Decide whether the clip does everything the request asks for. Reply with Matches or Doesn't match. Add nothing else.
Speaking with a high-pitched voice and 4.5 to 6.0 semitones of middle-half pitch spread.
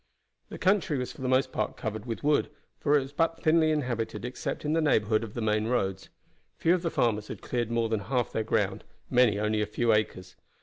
Doesn't match